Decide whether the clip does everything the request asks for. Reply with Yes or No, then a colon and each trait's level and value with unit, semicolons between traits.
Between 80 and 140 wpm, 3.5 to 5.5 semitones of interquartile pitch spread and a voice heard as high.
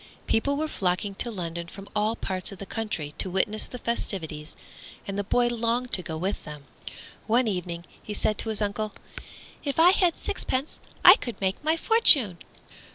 No: average, 180 wpm; average, 4.7 semitones; high, 210 Hz